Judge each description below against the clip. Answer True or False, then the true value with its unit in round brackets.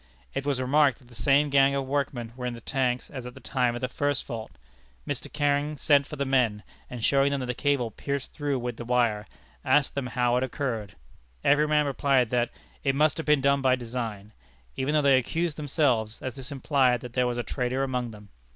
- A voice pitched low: True (130 Hz)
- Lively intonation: False (2.5 semitones)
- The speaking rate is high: True (220 wpm)